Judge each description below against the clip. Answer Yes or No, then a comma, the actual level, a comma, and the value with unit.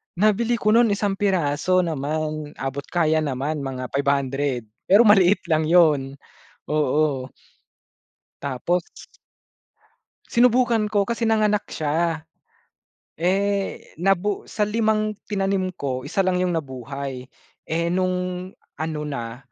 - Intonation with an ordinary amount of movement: No, wide, 6.0 semitones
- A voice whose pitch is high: No, medium, 170 Hz